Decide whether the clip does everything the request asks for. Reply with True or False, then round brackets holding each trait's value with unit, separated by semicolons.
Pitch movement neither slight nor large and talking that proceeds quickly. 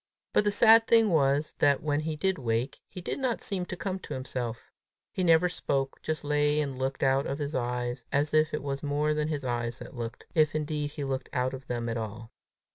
True (3.4 semitones; 230 wpm)